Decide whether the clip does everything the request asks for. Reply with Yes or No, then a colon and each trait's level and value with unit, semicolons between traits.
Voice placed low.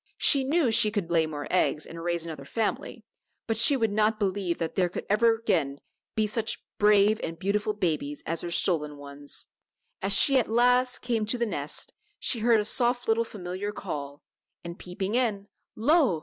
No: high, 205 Hz